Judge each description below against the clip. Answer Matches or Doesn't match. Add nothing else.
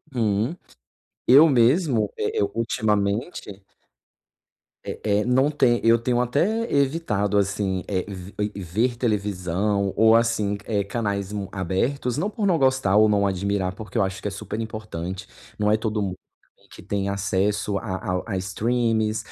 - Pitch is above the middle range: Doesn't match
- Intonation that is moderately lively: Matches